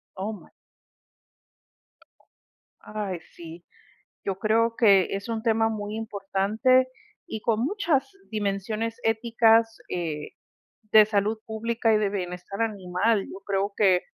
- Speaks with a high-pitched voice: Yes, high, 215 Hz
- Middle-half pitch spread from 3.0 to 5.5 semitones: No, narrow, 2.4 semitones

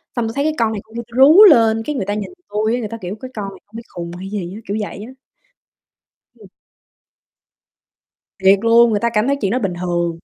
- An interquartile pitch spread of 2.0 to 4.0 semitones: Yes, average, 3.2 semitones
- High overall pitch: Yes, high, 220 Hz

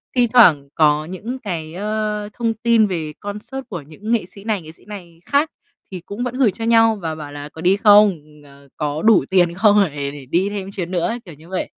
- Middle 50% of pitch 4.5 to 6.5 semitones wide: Yes, average, 5.3 semitones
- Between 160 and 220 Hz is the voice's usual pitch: Yes, high, 195 Hz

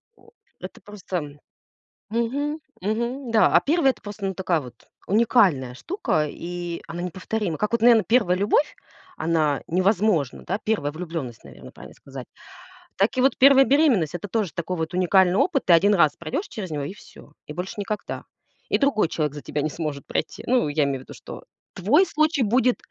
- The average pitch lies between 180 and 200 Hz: Yes, high, 190 Hz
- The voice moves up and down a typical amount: No, wide, 6.6 semitones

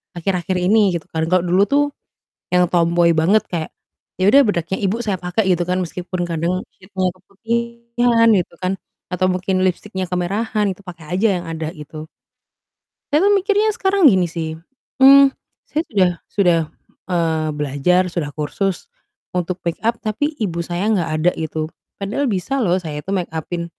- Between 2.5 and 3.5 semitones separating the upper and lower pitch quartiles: No, average, 3.9 semitones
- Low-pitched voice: No, medium, 185 Hz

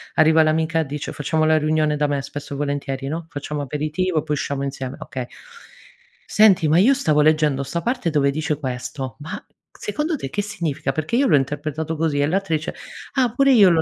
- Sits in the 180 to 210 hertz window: No, medium, 155 Hz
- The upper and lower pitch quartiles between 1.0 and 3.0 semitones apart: Yes, narrow, 2.6 semitones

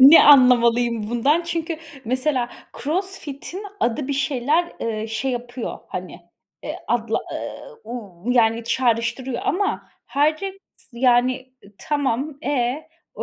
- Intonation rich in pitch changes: No, average, 4.1 semitones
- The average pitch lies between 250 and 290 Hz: Yes, very high, 255 Hz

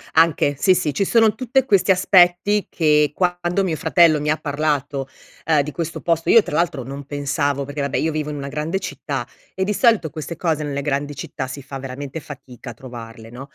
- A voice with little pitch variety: No, average, 3.9 semitones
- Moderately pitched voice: Yes, medium, 150 Hz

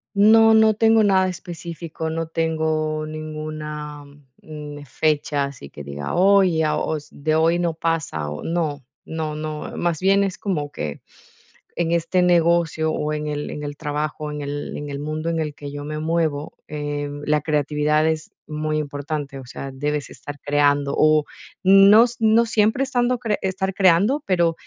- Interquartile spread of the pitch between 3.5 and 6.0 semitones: No, average, 2.9 semitones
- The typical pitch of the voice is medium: Yes, medium, 155 Hz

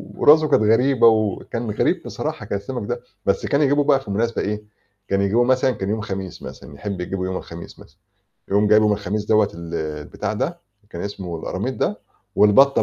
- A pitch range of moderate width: Yes, average, 3.8 semitones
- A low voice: Yes, low, 105 Hz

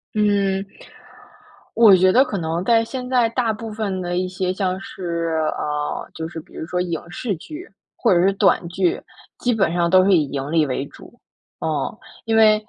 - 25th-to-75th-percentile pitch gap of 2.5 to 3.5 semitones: No, average, 4.6 semitones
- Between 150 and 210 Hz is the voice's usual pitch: Yes, high, 190 Hz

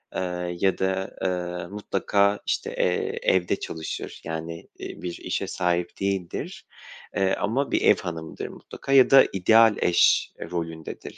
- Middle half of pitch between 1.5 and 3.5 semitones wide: Yes, narrow, 2.4 semitones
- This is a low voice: Yes, very low, 90 Hz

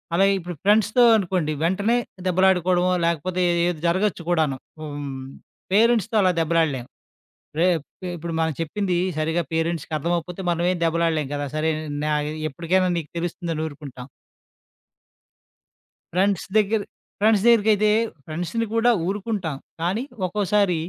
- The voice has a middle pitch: Yes, medium, 175 Hz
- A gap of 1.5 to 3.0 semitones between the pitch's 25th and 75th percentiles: No, average, 3.6 semitones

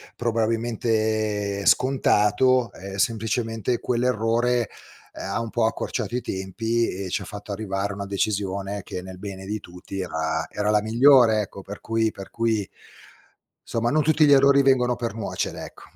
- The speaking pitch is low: Yes, low, 110 Hz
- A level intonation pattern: No, average, 3.1 semitones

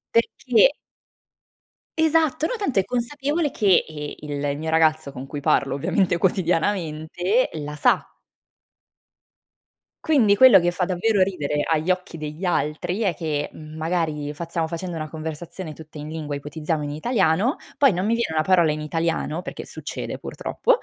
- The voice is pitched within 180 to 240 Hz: No, medium, 165 Hz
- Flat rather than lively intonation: No, average, 4.6 semitones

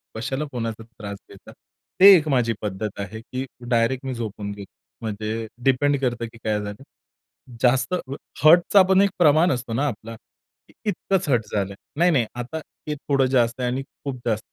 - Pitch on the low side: Yes, low, 125 Hz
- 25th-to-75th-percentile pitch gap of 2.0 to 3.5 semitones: No, average, 4.2 semitones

